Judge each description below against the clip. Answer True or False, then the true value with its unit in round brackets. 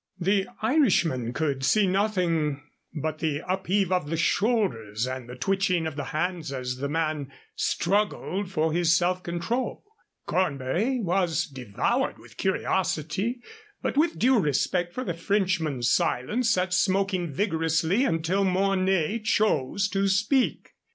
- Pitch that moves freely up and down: False (4.5 semitones)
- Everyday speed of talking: False (130 wpm)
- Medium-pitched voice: True (180 Hz)